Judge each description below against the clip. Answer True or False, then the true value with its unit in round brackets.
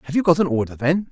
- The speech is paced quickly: True (325 wpm)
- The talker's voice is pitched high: False (155 Hz)